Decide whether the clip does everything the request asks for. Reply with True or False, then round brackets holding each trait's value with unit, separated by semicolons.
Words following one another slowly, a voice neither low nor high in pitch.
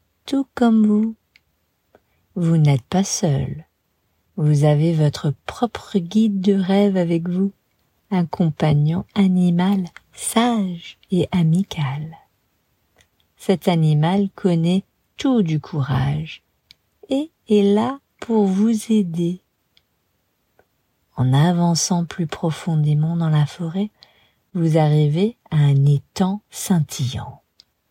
True (100 wpm; 170 Hz)